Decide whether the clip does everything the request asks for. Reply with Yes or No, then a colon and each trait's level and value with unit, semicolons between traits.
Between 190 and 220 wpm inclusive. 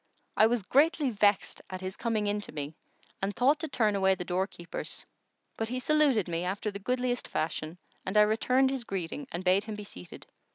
Yes: average, 200 wpm